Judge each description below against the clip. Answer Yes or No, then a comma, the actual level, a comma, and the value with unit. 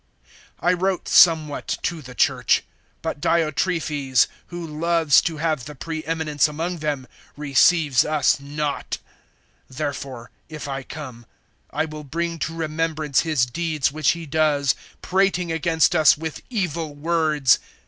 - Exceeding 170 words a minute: No, slow, 135 wpm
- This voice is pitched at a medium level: Yes, medium, 155 Hz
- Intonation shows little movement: Yes, narrow, 2.3 semitones